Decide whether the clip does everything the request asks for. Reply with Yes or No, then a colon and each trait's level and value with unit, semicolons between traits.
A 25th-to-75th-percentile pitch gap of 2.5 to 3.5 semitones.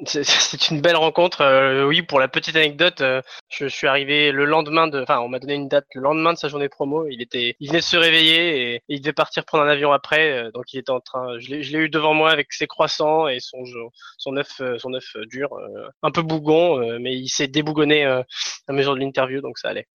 Yes: average, 3.2 semitones